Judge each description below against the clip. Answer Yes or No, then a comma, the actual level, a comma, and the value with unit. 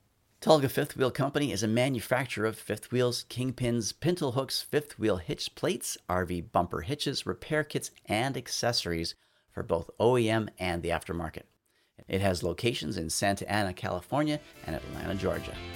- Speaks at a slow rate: No, average, 150 wpm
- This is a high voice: No, low, 110 Hz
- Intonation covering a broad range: Yes, wide, 6.2 semitones